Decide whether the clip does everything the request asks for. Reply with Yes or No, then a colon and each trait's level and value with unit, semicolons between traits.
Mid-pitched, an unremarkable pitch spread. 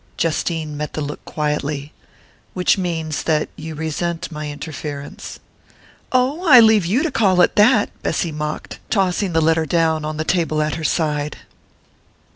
Yes: medium, 160 Hz; average, 3.1 semitones